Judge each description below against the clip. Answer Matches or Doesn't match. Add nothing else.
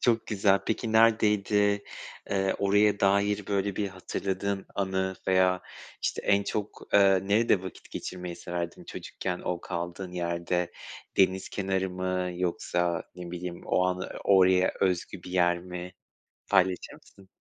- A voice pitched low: Matches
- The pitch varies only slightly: Matches